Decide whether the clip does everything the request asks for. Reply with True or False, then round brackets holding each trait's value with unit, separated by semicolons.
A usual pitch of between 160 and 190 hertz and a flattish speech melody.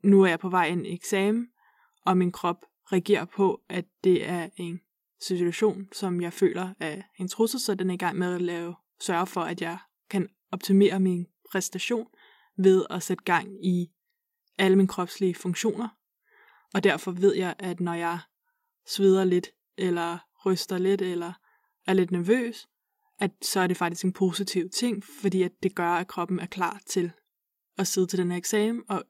True (185 Hz; 2.0 semitones)